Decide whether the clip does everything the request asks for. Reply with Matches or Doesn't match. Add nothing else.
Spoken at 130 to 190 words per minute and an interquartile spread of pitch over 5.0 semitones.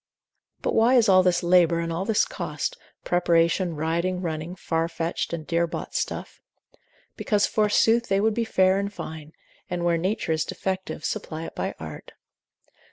Doesn't match